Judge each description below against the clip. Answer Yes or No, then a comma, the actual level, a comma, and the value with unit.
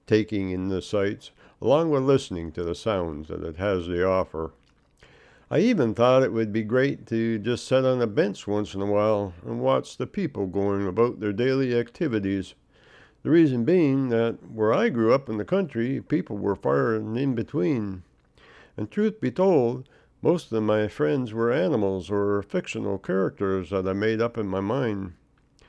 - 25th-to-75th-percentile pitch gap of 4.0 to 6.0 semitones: Yes, average, 4.4 semitones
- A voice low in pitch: Yes, low, 110 Hz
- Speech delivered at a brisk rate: No, average, 180 wpm